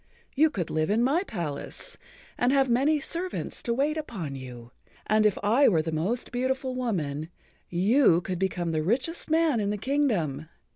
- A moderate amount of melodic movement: No, wide, 8.5 semitones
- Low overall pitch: No, high, 220 Hz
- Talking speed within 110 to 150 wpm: No, average, 175 wpm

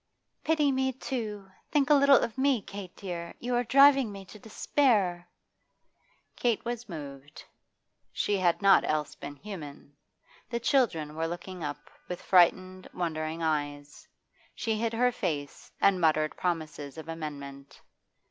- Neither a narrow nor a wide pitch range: No, wide, 7.1 semitones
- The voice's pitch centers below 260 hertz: Yes, medium, 185 Hz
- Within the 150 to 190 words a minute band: No, average, 140 wpm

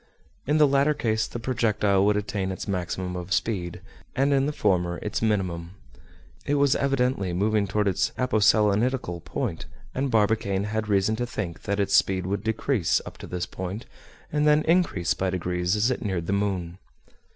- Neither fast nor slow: Yes, average, 175 wpm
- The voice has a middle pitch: No, low, 105 Hz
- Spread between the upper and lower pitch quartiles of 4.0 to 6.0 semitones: Yes, average, 4.7 semitones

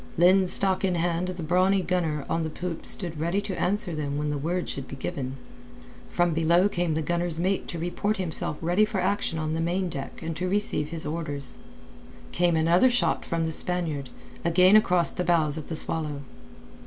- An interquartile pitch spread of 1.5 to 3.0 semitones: Yes, narrow, 2.5 semitones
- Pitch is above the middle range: No, medium, 170 Hz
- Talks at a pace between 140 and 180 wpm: No, average, 190 wpm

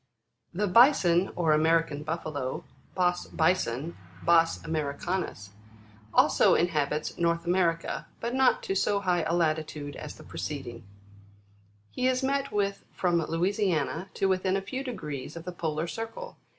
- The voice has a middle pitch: Yes, medium, 170 Hz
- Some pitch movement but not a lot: Yes, average, 3.8 semitones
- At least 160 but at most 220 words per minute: No, average, 145 wpm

